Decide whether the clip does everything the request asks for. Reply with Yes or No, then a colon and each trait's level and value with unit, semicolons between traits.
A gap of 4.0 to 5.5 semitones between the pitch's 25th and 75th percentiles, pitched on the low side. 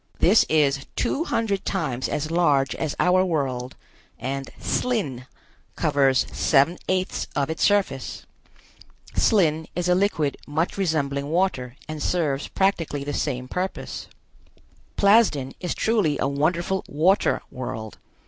No: average, 5.1 semitones; medium, 155 Hz